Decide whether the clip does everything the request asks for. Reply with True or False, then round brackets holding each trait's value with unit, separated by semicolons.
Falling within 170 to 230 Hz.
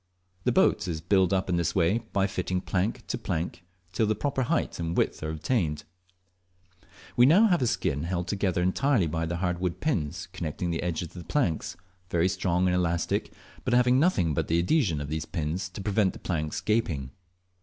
False (90 Hz)